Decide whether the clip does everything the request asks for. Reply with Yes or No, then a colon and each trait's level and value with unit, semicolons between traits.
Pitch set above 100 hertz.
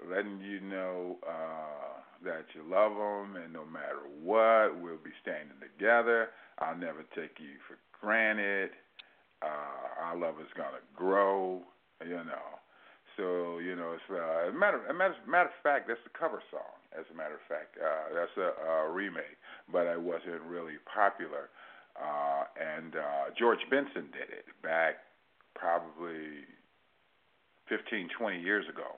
No: very low, 90 Hz